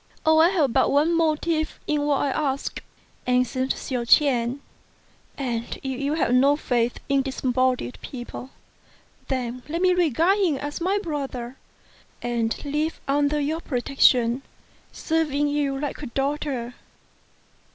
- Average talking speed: No, slow, 130 wpm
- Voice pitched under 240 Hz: No, very high, 280 Hz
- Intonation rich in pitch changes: No, average, 3.4 semitones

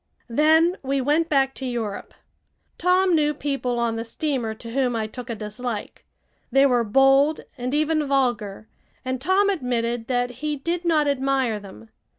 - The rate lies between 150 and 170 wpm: Yes, average, 160 wpm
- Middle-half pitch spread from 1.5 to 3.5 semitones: No, average, 4.2 semitones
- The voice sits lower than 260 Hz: No, very high, 265 Hz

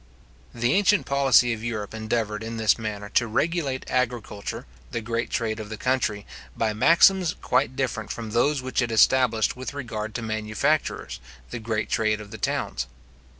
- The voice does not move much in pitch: No, average, 3.1 semitones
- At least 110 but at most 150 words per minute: No, average, 165 wpm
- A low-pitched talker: Yes, low, 115 Hz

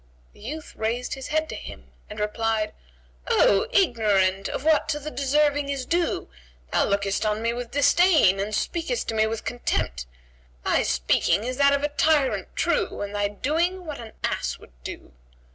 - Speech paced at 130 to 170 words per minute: No, average, 180 wpm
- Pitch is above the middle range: Yes, high, 245 Hz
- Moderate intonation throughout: No, wide, 6.1 semitones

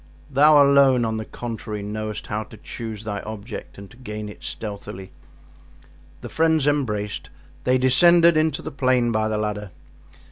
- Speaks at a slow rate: No, average, 155 wpm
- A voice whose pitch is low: Yes, low, 115 Hz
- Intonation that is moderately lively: Yes, average, 4.6 semitones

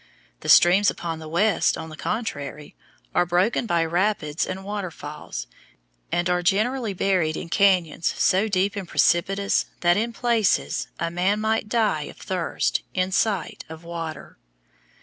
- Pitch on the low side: No, medium, 185 Hz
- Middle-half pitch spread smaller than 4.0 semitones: Yes, average, 3.6 semitones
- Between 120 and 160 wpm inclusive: Yes, average, 150 wpm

